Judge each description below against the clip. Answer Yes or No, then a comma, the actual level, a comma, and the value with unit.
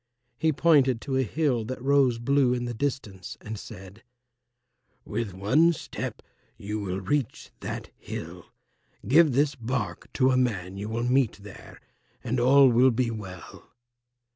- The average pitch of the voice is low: Yes, low, 125 Hz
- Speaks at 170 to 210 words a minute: No, average, 150 wpm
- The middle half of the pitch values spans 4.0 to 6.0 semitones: Yes, average, 4.3 semitones